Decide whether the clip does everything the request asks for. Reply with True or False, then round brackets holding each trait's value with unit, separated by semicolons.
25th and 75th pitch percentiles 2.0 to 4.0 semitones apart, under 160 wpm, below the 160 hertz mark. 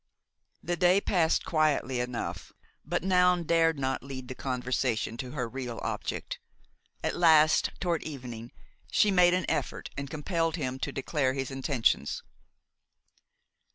False (4.6 semitones; 135 wpm; 140 Hz)